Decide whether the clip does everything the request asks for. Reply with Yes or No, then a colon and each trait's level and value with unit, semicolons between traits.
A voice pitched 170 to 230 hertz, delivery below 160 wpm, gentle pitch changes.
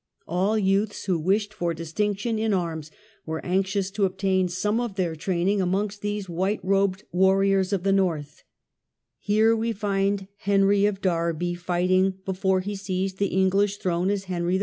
No: high, 190 Hz; average, 165 wpm; narrow, 2.0 semitones